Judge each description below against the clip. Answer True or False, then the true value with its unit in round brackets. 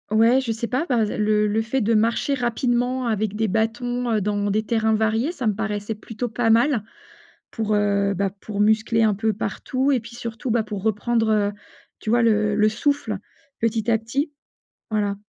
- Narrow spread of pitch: True (2.1 semitones)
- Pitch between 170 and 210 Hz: False (220 Hz)